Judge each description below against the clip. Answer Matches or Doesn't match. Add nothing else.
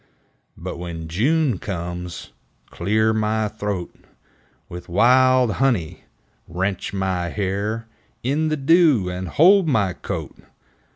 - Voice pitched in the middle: Doesn't match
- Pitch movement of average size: Doesn't match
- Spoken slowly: Matches